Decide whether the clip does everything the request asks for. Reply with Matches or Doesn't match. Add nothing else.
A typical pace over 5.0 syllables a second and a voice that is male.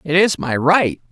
Doesn't match